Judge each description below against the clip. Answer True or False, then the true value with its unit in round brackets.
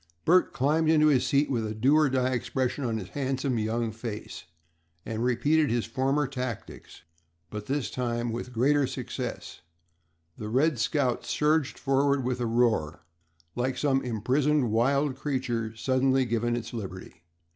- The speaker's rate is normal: True (150 wpm)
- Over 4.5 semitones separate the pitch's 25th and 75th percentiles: False (3.3 semitones)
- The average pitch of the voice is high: False (125 Hz)